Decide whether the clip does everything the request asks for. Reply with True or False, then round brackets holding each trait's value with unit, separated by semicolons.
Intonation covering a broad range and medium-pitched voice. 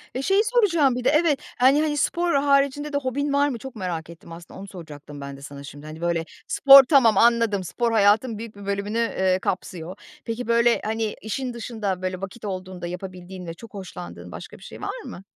False (6.5 semitones; 215 Hz)